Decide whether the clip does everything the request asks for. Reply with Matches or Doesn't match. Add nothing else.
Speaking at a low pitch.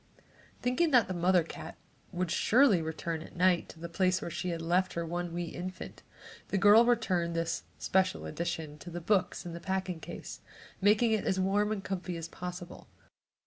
Doesn't match